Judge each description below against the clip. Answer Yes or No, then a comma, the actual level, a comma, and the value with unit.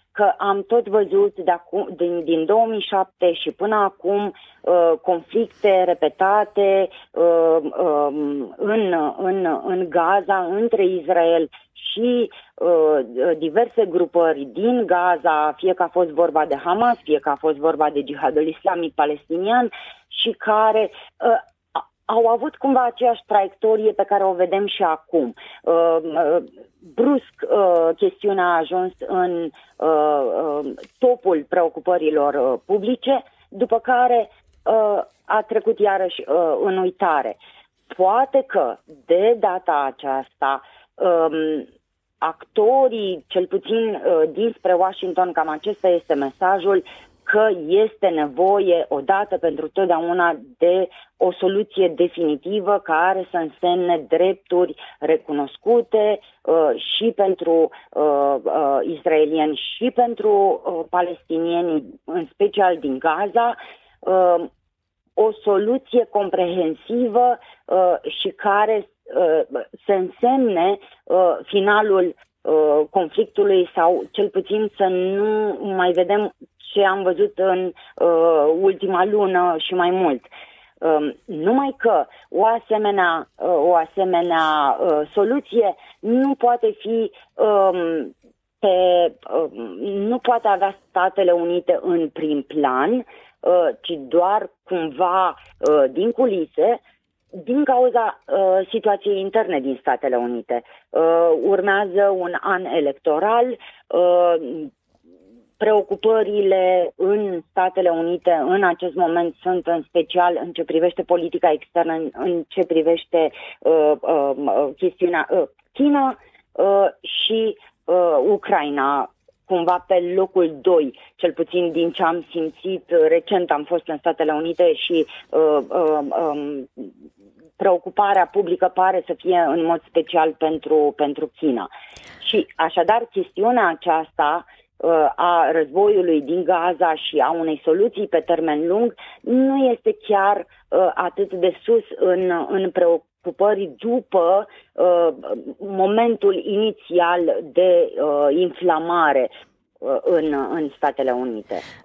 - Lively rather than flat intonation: No, average, 4.6 semitones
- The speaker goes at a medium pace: No, slow, 110 wpm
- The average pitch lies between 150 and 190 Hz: Yes, medium, 185 Hz